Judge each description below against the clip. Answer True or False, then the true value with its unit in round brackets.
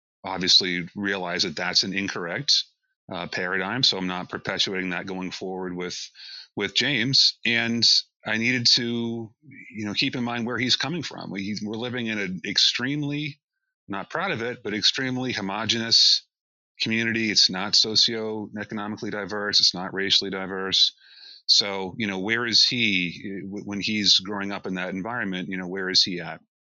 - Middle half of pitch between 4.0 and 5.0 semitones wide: False (3.5 semitones)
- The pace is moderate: True (160 wpm)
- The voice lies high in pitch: False (105 Hz)